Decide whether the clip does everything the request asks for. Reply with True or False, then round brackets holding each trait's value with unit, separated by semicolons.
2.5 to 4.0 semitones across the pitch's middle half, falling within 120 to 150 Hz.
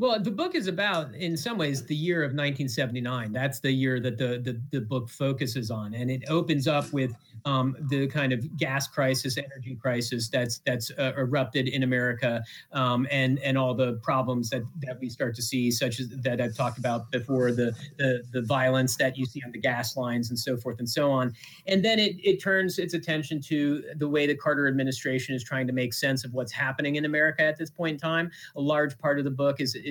True (2.8 semitones; 135 Hz)